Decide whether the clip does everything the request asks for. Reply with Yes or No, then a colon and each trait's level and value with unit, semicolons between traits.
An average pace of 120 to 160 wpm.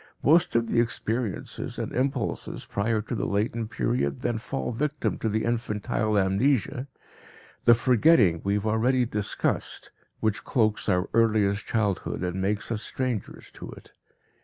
Yes: average, 145 wpm